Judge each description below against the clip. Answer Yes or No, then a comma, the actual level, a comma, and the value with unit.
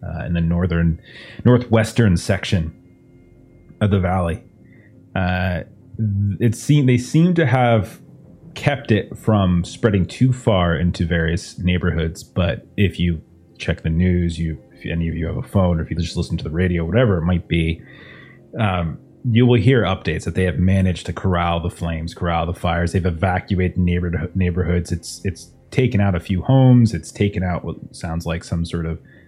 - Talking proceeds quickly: No, average, 175 wpm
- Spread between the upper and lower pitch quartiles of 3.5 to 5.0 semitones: Yes, average, 3.9 semitones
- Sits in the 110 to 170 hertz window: No, very low, 90 Hz